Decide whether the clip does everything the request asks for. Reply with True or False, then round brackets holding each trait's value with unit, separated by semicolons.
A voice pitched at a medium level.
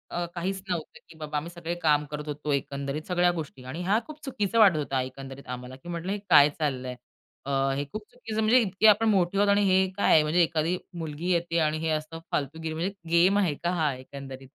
True (165 Hz)